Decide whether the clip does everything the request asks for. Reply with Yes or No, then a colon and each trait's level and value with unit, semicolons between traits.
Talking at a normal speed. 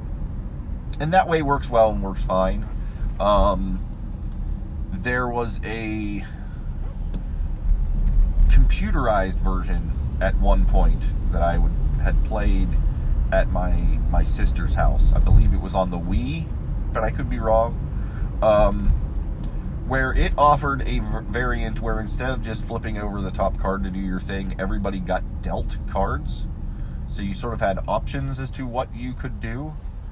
Yes: average, 145 wpm